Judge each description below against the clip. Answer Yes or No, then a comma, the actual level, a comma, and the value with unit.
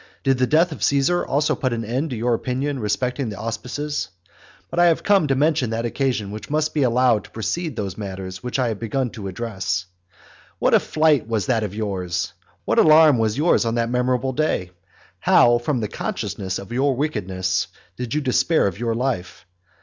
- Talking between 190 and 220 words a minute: Yes, average, 195 wpm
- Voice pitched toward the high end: No, low, 125 Hz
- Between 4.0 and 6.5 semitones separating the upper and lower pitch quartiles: Yes, average, 5.0 semitones